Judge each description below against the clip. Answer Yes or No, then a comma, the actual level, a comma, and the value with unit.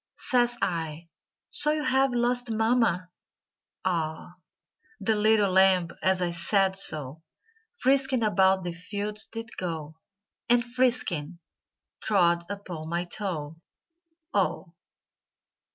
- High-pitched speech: Yes, high, 195 Hz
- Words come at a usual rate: No, slow, 105 wpm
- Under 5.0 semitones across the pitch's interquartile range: No, wide, 5.4 semitones